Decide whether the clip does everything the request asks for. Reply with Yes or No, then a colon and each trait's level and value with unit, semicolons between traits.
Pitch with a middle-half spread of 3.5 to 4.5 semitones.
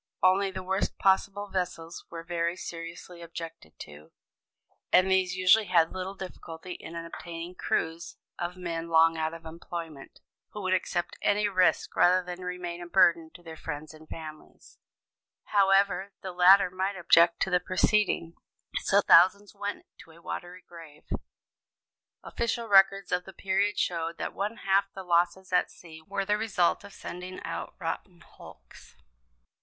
No: narrow, 2.5 semitones